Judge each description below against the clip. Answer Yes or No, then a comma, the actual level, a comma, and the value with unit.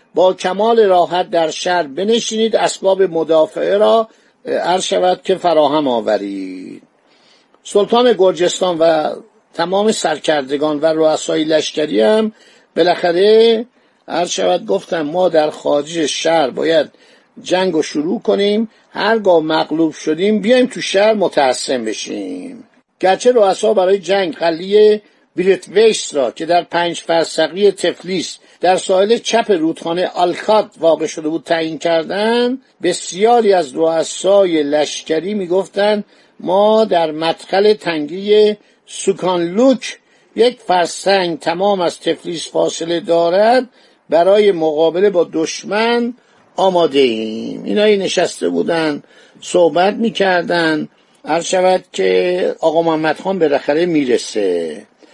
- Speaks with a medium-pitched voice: Yes, medium, 180 Hz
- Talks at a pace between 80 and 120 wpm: Yes, average, 110 wpm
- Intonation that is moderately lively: Yes, average, 4.6 semitones